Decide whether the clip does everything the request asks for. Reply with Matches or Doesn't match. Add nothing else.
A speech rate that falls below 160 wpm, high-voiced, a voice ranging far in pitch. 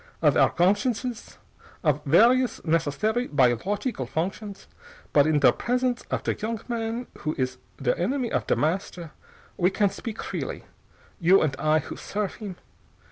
Matches